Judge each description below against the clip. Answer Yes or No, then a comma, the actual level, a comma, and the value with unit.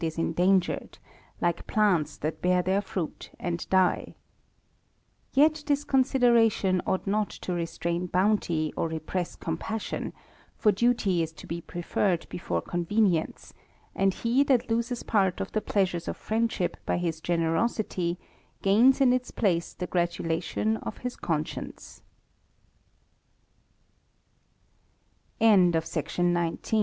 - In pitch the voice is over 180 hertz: Yes, high, 190 Hz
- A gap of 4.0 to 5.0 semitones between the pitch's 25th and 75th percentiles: Yes, average, 4.6 semitones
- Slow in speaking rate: Yes, slow, 120 wpm